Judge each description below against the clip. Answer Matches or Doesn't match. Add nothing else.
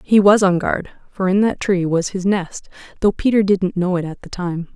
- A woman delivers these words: Matches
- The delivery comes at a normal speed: Doesn't match